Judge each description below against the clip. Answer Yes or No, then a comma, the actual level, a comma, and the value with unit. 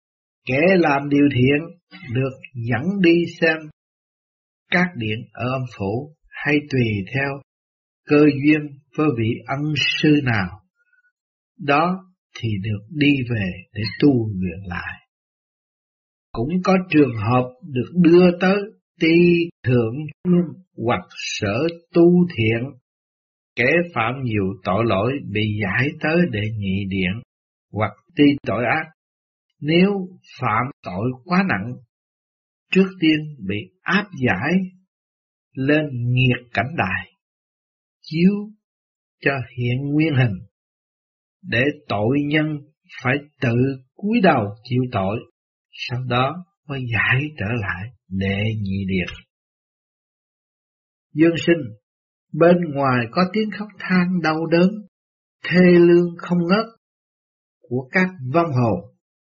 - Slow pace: Yes, slow, 115 wpm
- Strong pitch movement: Yes, wide, 7.2 semitones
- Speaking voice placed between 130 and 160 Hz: Yes, medium, 140 Hz